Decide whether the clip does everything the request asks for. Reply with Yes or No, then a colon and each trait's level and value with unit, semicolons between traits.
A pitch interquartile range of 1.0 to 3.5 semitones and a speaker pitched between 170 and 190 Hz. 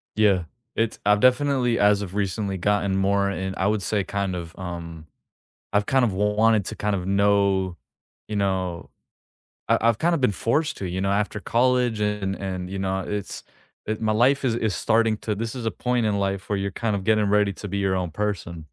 No: narrow, 2.4 semitones; low, 100 Hz